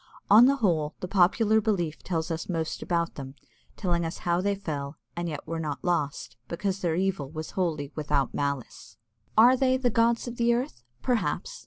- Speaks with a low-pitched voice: No, medium, 175 Hz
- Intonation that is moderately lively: No, wide, 5.8 semitones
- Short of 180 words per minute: No, average, 185 wpm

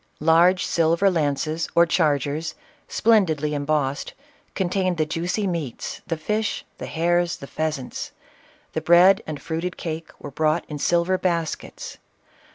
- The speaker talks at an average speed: No, slow, 130 wpm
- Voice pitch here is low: No, medium, 165 Hz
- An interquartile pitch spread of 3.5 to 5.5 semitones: No, narrow, 2.6 semitones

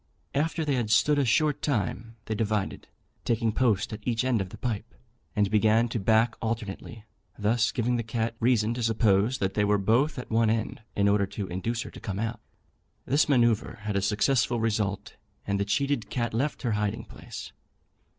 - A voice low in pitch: Yes, low, 110 Hz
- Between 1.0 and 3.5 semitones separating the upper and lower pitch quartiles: Yes, narrow, 2.6 semitones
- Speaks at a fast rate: No, average, 190 wpm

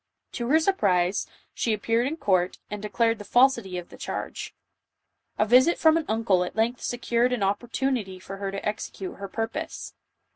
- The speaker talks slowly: No, average, 180 wpm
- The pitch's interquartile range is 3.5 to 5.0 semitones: Yes, average, 4.1 semitones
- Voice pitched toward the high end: Yes, high, 225 Hz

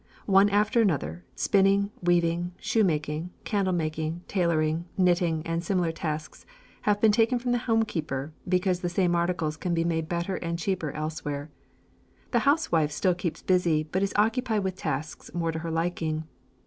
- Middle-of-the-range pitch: Yes, medium, 175 Hz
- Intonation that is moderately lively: Yes, average, 3.5 semitones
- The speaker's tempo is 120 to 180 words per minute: Yes, average, 155 wpm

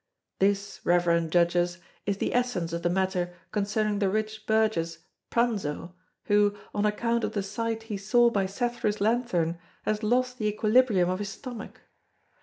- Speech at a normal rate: Yes, average, 155 wpm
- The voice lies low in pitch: No, high, 205 Hz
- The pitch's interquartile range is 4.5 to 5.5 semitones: No, average, 3.6 semitones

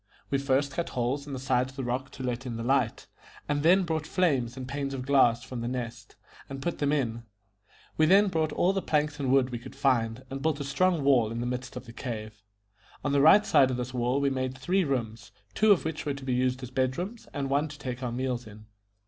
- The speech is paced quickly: Yes, fast, 250 wpm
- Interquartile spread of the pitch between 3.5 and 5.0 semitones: No, average, 2.7 semitones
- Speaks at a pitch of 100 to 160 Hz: Yes, low, 135 Hz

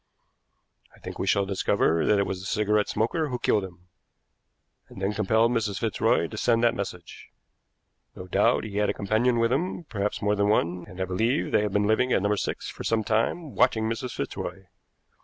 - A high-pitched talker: No, low, 105 Hz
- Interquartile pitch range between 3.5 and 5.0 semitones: No, average, 3.0 semitones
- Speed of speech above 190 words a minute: Yes, average, 200 wpm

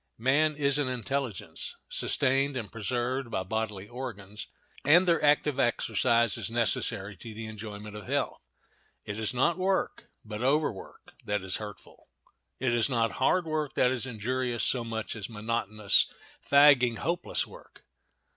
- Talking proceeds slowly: No, average, 145 wpm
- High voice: No, low, 120 Hz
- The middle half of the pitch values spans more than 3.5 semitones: Yes, average, 4.2 semitones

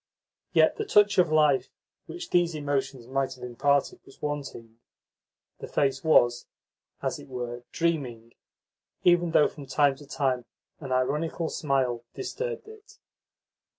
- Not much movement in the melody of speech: No, average, 4.5 semitones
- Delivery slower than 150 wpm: Yes, slow, 135 wpm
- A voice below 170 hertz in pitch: Yes, medium, 140 Hz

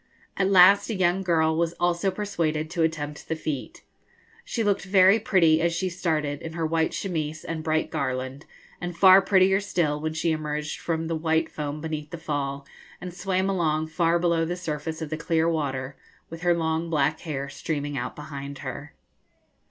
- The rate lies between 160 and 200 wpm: Yes, average, 180 wpm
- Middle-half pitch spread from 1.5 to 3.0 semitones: Yes, average, 2.7 semitones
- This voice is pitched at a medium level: Yes, medium, 160 Hz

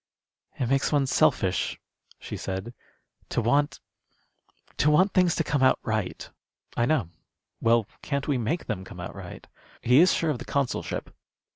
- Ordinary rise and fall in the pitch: Yes, average, 4.4 semitones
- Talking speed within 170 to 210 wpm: No, average, 160 wpm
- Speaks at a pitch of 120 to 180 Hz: Yes, low, 135 Hz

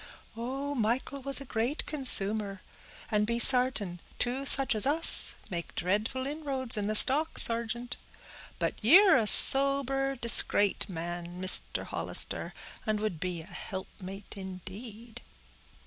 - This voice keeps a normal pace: No, slow, 130 wpm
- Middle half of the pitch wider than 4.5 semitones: Yes, average, 5.3 semitones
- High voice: Yes, high, 230 Hz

